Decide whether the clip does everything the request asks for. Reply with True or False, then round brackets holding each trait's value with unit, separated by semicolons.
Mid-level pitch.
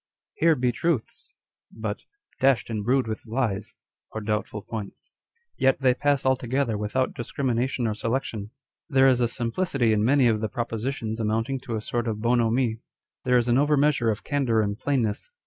False (120 Hz)